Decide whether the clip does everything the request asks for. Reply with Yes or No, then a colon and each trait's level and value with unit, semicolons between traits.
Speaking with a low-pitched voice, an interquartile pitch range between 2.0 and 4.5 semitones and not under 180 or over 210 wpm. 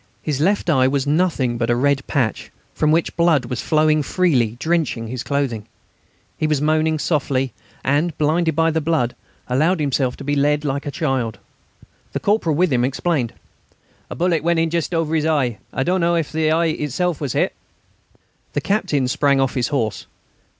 No: medium, 150 Hz; average, 3.6 semitones; average, 185 wpm